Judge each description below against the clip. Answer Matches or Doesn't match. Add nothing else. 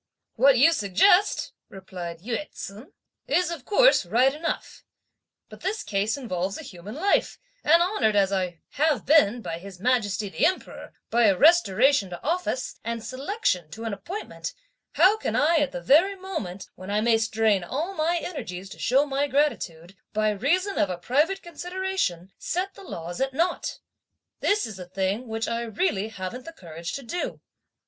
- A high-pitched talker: Matches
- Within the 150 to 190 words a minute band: Matches